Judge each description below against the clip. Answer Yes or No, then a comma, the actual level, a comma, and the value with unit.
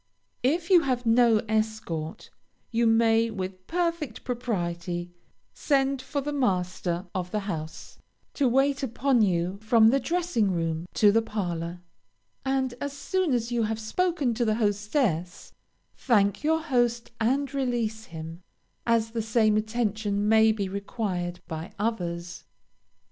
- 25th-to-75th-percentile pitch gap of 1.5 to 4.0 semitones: No, average, 5.2 semitones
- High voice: Yes, high, 220 Hz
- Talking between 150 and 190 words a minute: No, average, 140 wpm